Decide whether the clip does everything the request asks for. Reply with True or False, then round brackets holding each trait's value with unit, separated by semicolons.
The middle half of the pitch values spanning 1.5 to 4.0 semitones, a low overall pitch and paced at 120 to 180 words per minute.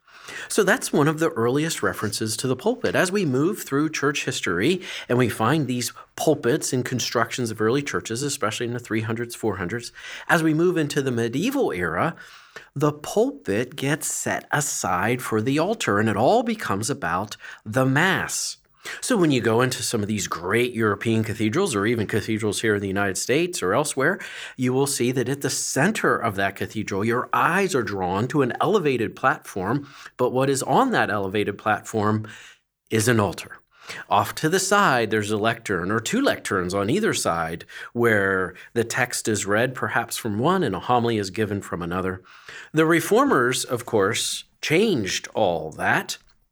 False (4.9 semitones; 120 Hz; 175 wpm)